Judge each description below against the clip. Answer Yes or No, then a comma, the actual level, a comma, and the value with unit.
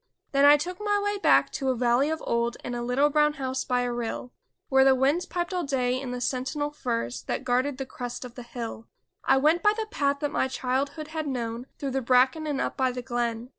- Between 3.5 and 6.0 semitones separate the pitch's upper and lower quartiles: No, average, 3.1 semitones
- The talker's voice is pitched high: Yes, very high, 265 Hz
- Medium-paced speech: No, fast, 240 wpm